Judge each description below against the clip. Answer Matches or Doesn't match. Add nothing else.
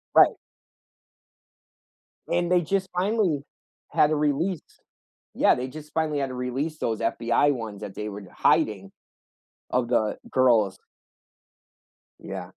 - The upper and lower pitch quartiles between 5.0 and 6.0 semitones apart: Matches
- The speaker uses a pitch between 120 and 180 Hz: Matches